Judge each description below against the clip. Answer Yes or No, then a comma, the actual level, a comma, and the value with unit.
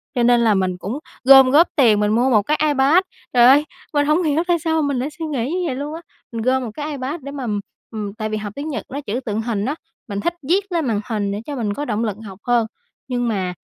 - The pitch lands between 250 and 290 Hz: Yes, very high, 255 Hz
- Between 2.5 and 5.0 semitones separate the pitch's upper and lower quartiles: No, wide, 5.4 semitones